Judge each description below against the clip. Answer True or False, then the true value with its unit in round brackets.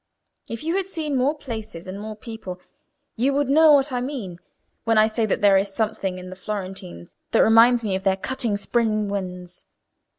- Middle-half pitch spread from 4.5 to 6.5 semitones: True (4.8 semitones)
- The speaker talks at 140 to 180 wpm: False (195 wpm)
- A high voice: True (215 Hz)